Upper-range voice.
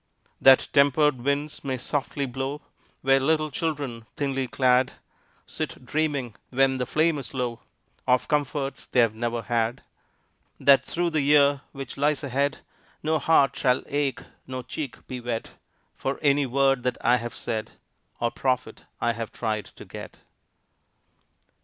No: low, 135 Hz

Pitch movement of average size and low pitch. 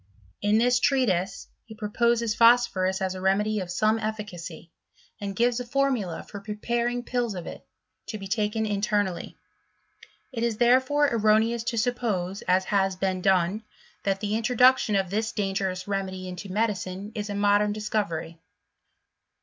No: average, 3.4 semitones; high, 210 Hz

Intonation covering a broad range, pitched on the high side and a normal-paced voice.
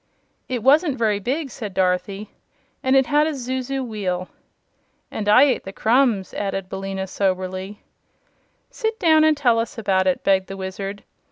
Yes: wide, 5.7 semitones; high, 210 Hz; average, 160 wpm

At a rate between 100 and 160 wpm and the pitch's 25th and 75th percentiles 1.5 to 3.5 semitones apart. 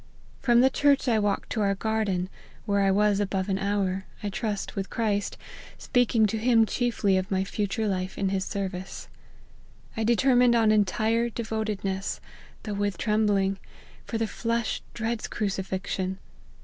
Yes: average, 155 wpm; average, 2.7 semitones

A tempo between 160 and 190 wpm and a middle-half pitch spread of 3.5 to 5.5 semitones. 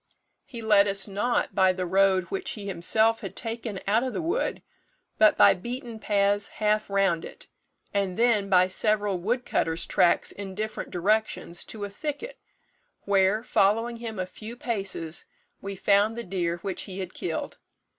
No: average, 165 wpm; average, 2.9 semitones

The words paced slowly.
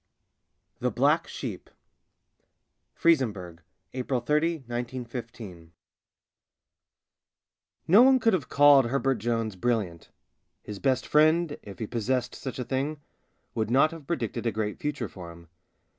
Yes: slow, 130 wpm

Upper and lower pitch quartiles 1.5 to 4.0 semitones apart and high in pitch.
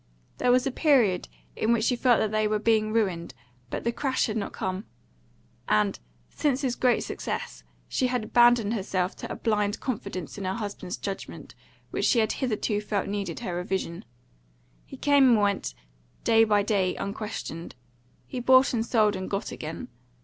Yes: average, 3.5 semitones; high, 215 Hz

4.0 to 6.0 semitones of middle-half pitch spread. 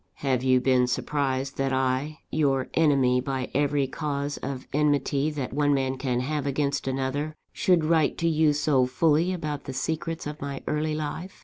No: narrow, 2.4 semitones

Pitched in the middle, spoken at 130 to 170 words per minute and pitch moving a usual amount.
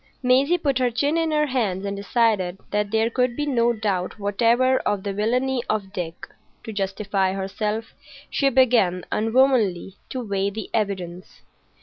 No: high, 220 Hz; average, 155 wpm; average, 4.4 semitones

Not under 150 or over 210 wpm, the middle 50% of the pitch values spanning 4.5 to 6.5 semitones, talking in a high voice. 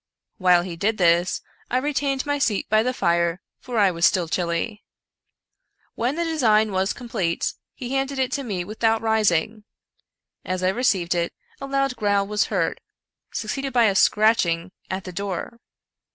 Yes: average, 165 wpm; wide, 5.5 semitones; high, 210 Hz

